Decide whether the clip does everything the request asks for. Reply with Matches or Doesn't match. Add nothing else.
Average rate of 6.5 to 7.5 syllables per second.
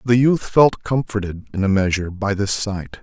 Doesn't match